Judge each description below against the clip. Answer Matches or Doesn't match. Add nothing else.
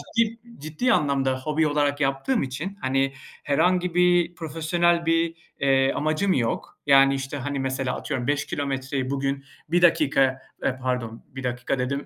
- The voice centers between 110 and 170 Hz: Matches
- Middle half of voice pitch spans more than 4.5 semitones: Doesn't match